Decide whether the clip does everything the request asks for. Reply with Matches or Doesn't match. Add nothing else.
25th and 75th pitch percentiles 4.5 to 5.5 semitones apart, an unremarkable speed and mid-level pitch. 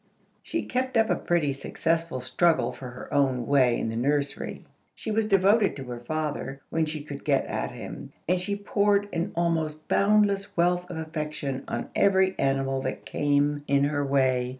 Matches